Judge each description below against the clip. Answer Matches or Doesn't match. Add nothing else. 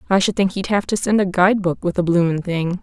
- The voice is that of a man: Doesn't match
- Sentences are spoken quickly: Matches